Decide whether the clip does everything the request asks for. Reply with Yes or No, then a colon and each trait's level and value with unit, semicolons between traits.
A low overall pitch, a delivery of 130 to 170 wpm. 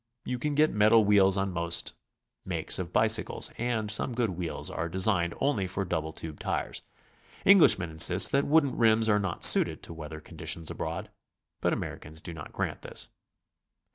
Yes: very low, 95 Hz; average, 165 wpm